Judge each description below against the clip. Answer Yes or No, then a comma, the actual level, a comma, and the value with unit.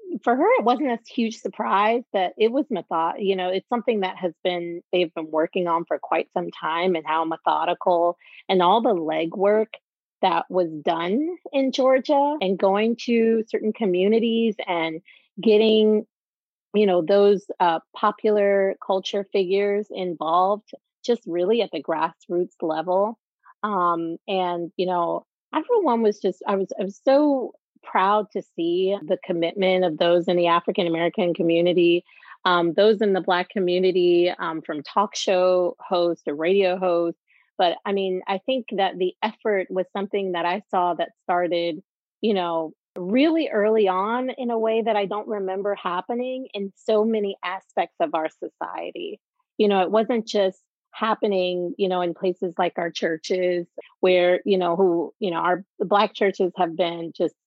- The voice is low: No, high, 190 Hz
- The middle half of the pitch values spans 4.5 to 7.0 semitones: No, average, 3.5 semitones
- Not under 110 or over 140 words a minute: No, average, 165 wpm